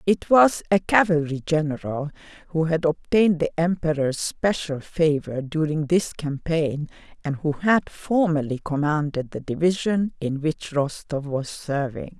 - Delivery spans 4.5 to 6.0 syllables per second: No, 4.3 syllables/s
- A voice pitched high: No, medium, 160 Hz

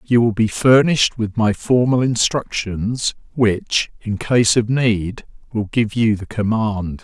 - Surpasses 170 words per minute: No, average, 155 wpm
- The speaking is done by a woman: No, male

